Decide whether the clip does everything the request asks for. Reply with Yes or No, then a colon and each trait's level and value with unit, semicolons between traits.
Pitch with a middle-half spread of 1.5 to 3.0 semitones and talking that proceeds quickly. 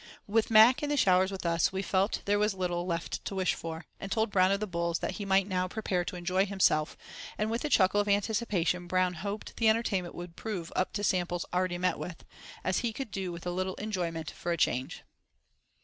Yes: average, 2.7 semitones; fast, 225 wpm